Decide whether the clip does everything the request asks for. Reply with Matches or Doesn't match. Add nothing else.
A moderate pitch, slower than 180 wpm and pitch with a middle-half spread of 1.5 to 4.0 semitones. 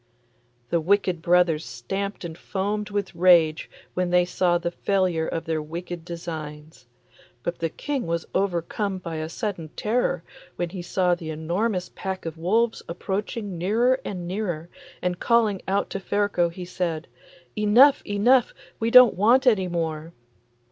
Matches